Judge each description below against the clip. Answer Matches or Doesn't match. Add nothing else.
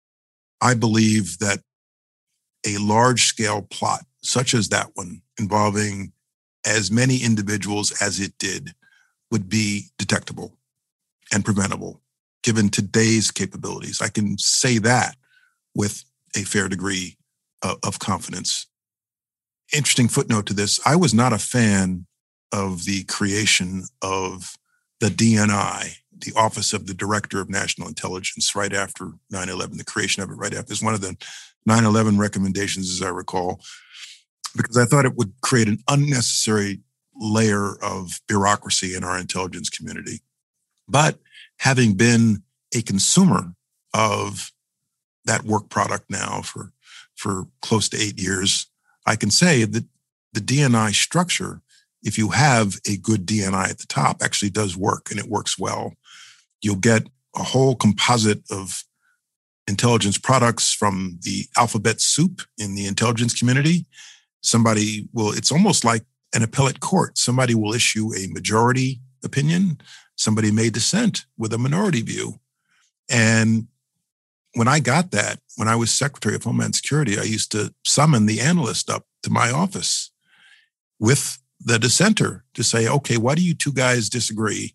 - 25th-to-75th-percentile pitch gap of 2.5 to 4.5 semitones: Matches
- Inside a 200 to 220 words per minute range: Doesn't match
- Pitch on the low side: Matches